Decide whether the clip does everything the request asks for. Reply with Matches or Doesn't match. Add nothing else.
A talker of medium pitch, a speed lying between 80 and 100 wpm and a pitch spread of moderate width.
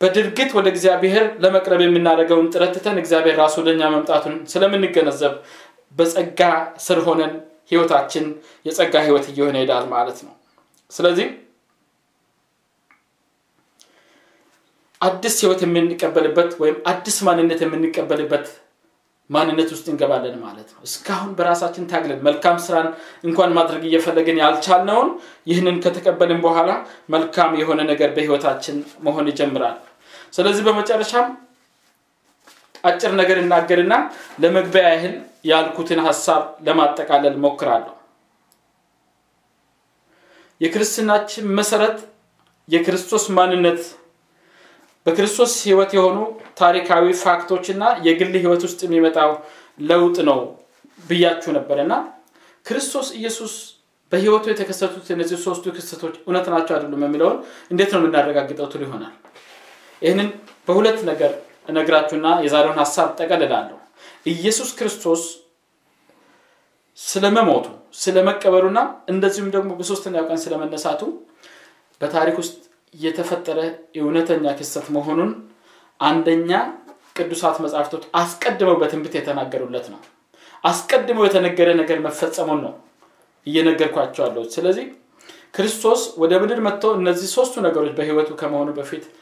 Matches